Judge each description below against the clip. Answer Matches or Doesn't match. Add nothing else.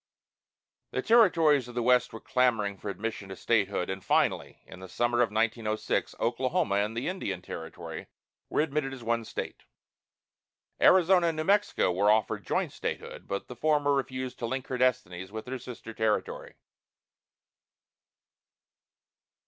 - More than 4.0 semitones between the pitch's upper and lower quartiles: Matches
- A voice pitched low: Matches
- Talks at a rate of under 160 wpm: Matches